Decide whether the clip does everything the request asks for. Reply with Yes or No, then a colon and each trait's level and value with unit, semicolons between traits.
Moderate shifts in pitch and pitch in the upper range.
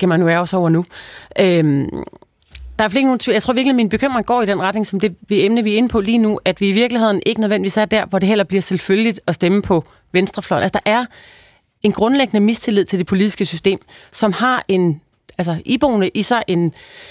Yes: average, 3.5 semitones; high, 205 Hz